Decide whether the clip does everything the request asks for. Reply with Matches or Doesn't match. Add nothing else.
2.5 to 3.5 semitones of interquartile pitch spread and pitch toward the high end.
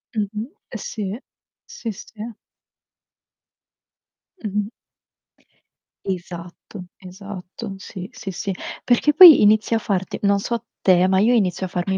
Matches